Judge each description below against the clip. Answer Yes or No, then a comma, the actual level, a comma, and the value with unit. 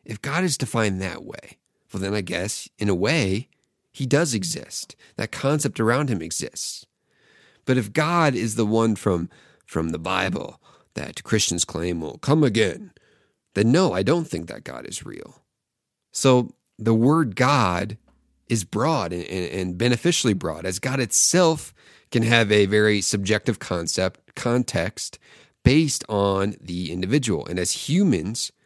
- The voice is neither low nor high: No, low, 110 Hz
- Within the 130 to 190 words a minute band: Yes, average, 155 wpm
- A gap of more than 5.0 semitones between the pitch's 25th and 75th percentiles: Yes, wide, 5.6 semitones